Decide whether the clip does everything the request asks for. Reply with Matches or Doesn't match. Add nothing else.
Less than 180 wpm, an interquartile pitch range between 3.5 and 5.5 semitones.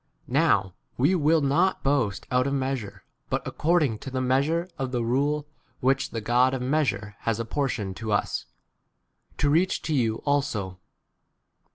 Doesn't match